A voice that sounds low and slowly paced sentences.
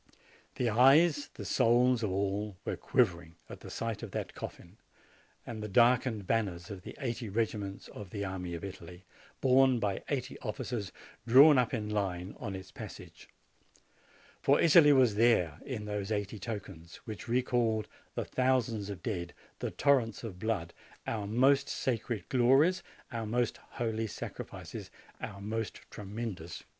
No: low, 110 Hz; average, 150 wpm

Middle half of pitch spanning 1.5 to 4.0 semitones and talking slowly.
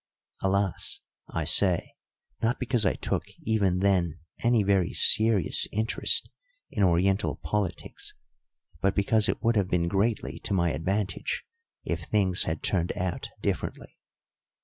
Yes: average, 2.9 semitones; slow, 130 wpm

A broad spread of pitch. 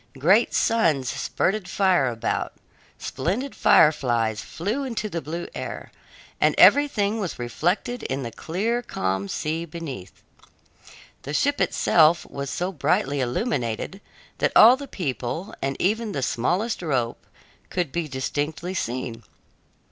Yes: wide, 7.6 semitones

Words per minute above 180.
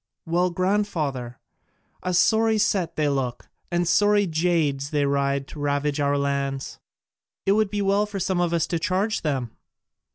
No: average, 160 wpm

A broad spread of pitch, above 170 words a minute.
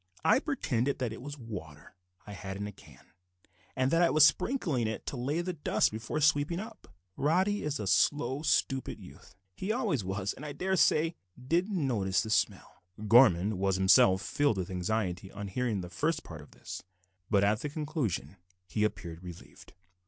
Yes: wide, 8.0 semitones; average, 180 wpm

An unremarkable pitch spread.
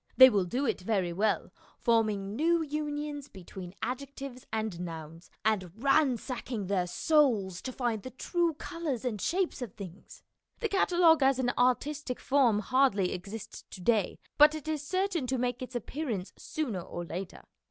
No: wide, 6.6 semitones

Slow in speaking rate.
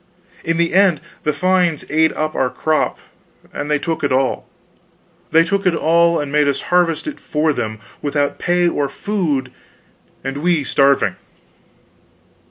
No: average, 155 wpm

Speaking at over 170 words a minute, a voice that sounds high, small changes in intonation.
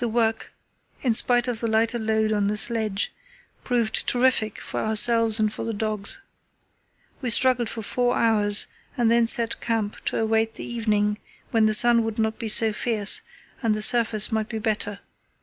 Yes: average, 180 wpm; high, 225 Hz; narrow, 1.5 semitones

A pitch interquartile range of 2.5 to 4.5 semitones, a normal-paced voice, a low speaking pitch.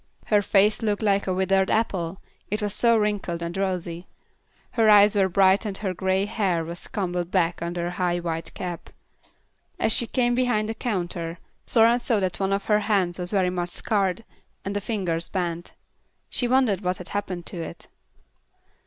No: average, 3.1 semitones; average, 180 wpm; high, 195 Hz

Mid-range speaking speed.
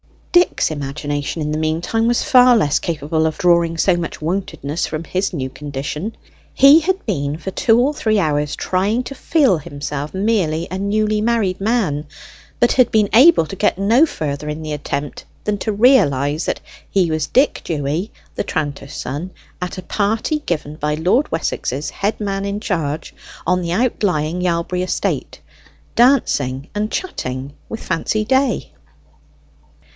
Yes: average, 160 wpm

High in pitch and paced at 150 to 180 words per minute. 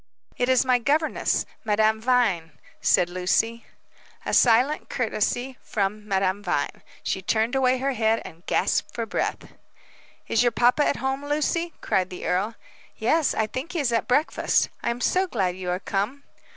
Yes: high, 230 Hz; average, 165 wpm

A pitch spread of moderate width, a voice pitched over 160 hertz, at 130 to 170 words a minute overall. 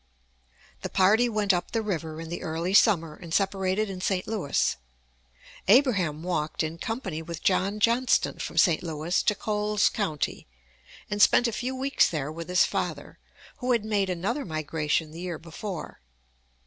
Yes: average, 4.6 semitones; medium, 185 Hz; average, 160 wpm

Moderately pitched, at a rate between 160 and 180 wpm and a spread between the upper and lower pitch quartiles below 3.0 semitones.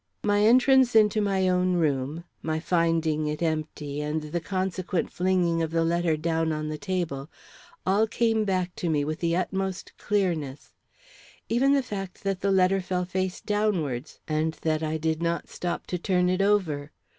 No: medium, 175 Hz; average, 170 wpm; average, 3.5 semitones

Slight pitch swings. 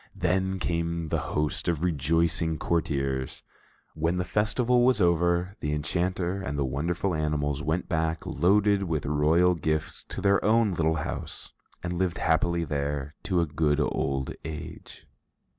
No: average, 3.1 semitones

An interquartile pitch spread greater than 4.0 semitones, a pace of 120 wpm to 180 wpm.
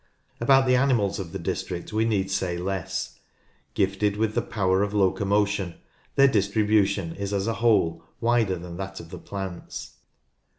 No: narrow, 2.4 semitones; average, 155 wpm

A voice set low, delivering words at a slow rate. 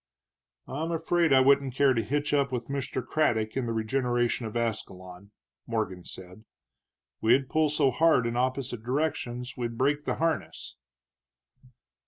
No: low, 130 Hz; average, 145 wpm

